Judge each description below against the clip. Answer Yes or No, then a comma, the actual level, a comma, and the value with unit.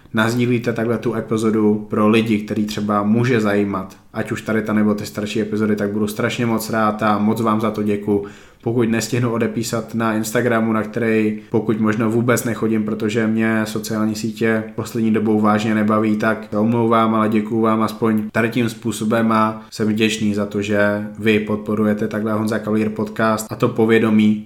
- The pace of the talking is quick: Yes, fast, 180 wpm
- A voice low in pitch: Yes, low, 110 Hz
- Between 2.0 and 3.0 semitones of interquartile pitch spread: No, narrow, 0.9 semitones